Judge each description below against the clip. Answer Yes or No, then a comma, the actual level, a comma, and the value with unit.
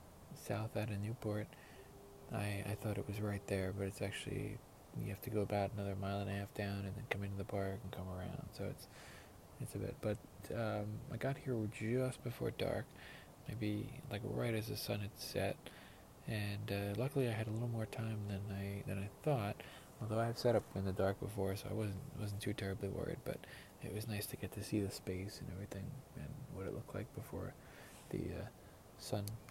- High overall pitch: No, low, 105 Hz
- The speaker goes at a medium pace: No, fast, 215 wpm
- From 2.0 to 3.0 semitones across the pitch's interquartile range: Yes, narrow, 2.4 semitones